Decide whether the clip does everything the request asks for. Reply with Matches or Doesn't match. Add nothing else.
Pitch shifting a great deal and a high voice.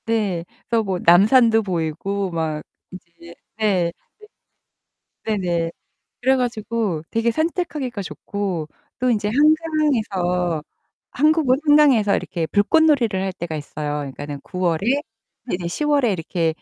Matches